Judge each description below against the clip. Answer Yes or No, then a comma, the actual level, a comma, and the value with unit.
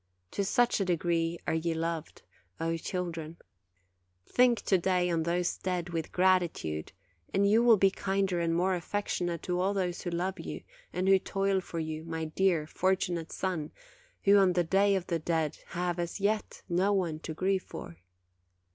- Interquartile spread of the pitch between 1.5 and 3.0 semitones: Yes, narrow, 2.5 semitones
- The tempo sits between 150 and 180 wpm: Yes, average, 175 wpm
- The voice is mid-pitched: Yes, medium, 180 Hz